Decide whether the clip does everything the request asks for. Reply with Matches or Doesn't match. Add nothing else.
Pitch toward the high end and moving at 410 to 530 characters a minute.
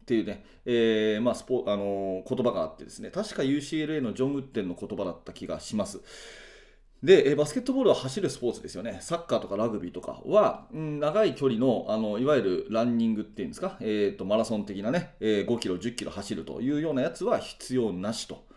Doesn't match